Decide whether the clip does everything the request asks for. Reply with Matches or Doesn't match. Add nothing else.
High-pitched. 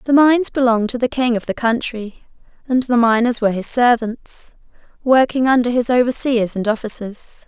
Matches